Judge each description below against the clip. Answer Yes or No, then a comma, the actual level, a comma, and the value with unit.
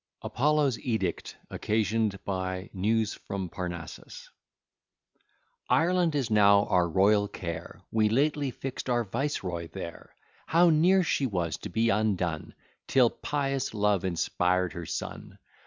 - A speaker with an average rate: No, slow, 125 wpm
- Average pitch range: No, wide, 6.2 semitones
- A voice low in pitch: Yes, low, 105 Hz